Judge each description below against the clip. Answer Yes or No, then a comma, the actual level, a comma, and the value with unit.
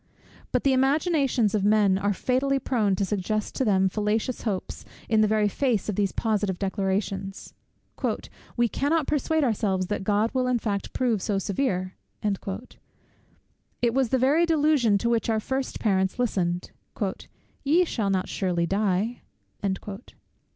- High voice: Yes, high, 215 Hz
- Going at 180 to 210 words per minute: No, average, 145 wpm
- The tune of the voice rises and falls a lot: No, average, 4.7 semitones